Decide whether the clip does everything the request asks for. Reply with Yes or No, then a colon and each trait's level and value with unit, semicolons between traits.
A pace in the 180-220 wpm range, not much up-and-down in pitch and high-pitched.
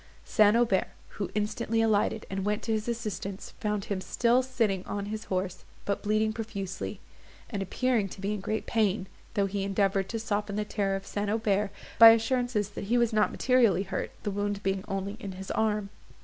Yes: average, 190 wpm; narrow, 2.1 semitones; high, 210 Hz